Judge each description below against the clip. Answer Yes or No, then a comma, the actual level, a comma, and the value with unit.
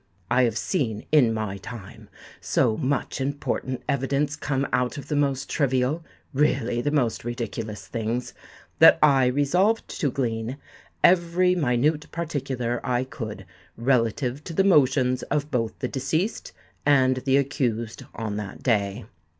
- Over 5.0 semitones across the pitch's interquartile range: No, average, 3.6 semitones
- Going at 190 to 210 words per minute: No, slow, 135 wpm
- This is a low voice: Yes, low, 130 Hz